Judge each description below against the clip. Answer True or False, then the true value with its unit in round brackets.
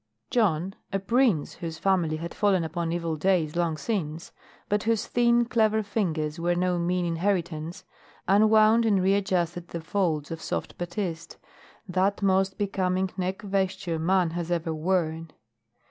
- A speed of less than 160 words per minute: True (145 wpm)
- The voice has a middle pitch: True (180 Hz)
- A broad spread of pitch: False (3.2 semitones)